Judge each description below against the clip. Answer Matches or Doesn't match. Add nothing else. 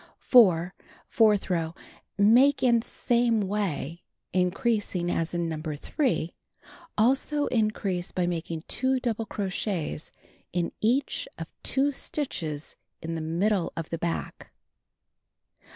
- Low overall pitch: Doesn't match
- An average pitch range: Doesn't match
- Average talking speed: Doesn't match